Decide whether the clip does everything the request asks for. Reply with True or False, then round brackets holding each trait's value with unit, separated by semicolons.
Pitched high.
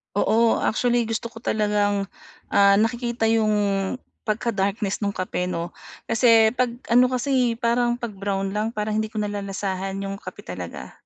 True (215 Hz)